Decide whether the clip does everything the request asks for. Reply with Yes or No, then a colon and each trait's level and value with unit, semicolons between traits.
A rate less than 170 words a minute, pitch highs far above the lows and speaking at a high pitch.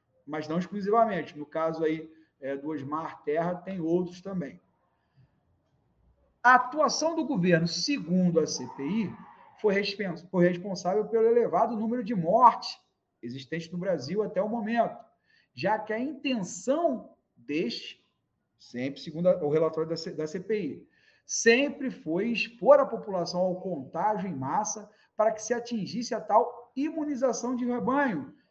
Yes: average, 135 wpm; wide, 6.0 semitones; high, 200 Hz